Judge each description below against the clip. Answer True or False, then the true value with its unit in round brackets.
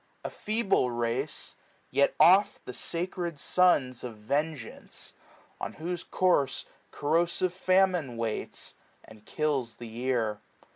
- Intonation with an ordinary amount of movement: False (6.8 semitones)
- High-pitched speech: False (145 Hz)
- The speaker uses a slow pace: True (110 wpm)